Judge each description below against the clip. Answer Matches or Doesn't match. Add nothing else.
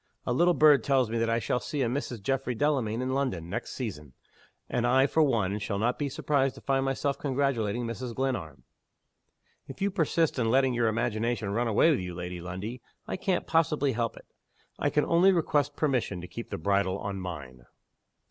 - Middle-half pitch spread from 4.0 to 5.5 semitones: Matches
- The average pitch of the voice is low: Matches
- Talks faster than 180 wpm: Matches